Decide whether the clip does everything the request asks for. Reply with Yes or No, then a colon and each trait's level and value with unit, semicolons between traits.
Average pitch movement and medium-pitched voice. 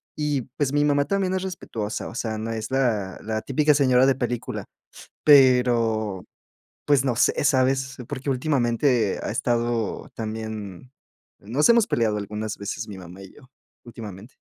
No: average, 4.0 semitones; low, 120 Hz